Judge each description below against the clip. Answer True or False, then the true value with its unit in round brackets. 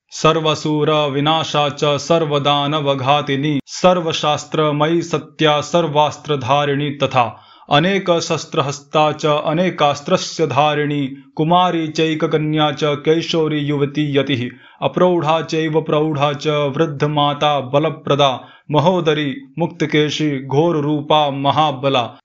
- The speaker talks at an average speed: False (65 wpm)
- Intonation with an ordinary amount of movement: False (1.7 semitones)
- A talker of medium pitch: True (150 Hz)